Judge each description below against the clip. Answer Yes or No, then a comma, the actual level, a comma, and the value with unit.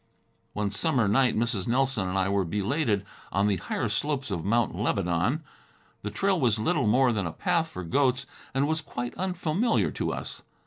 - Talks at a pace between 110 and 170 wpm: No, average, 180 wpm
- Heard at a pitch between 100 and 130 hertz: Yes, low, 120 Hz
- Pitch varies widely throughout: Yes, wide, 6.2 semitones